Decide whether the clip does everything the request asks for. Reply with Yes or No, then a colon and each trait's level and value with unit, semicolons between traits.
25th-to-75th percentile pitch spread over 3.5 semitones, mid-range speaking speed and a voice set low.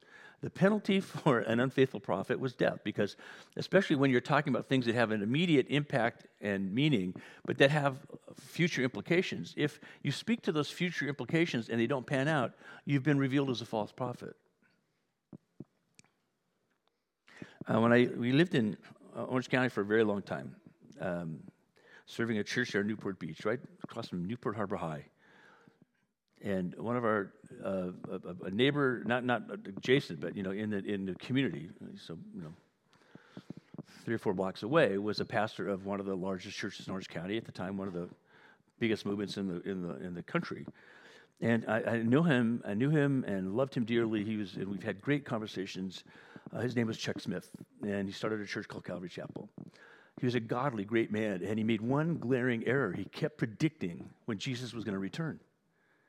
Yes: wide, 5.6 semitones; average, 190 wpm; low, 120 Hz